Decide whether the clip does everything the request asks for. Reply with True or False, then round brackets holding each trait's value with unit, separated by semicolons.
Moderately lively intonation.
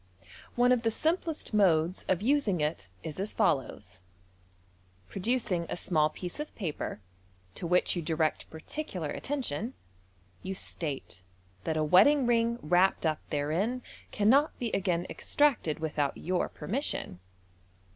False (7.2 semitones)